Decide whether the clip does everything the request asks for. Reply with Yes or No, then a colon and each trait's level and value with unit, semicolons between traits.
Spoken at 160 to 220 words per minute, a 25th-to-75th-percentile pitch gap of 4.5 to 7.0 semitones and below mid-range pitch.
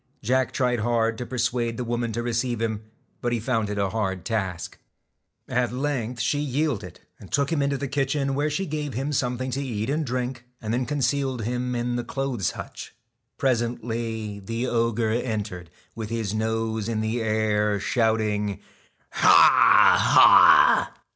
No: average, 165 wpm; average, 2.9 semitones; low, 120 Hz